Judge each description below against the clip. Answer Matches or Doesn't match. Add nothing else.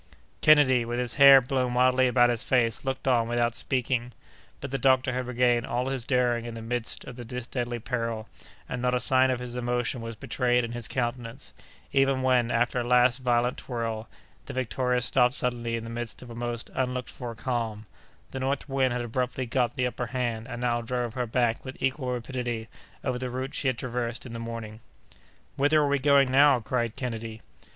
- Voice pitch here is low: Matches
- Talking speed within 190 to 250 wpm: Matches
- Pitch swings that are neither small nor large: Doesn't match